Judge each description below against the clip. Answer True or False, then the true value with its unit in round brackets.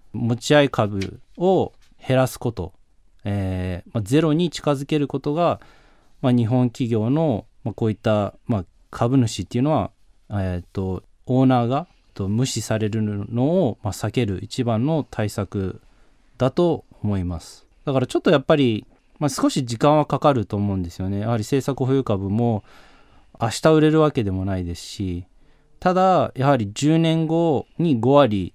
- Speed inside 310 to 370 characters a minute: False (300 characters per minute)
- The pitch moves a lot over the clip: True (5.9 semitones)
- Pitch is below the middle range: True (120 Hz)